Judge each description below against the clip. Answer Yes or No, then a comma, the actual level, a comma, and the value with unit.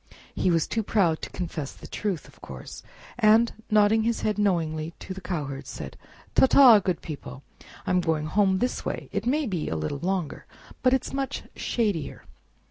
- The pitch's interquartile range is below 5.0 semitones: No, wide, 5.5 semitones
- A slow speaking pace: No, average, 185 wpm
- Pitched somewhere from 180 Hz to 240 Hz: Yes, high, 190 Hz